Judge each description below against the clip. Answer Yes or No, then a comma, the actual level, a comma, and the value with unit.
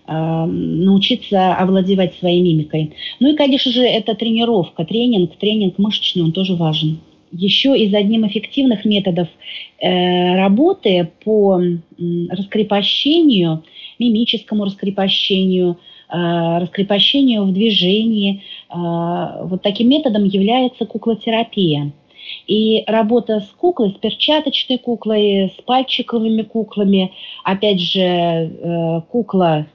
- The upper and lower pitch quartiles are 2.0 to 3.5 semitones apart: No, average, 4.2 semitones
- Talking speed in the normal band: No, slow, 105 wpm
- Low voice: No, high, 200 Hz